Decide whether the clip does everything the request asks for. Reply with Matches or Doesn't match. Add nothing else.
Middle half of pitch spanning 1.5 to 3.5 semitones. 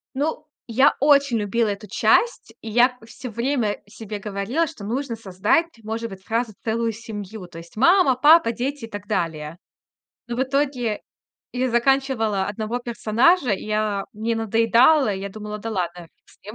Doesn't match